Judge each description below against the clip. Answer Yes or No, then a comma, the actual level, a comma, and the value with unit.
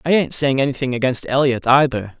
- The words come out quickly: No, average, 190 wpm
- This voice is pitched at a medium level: No, low, 130 Hz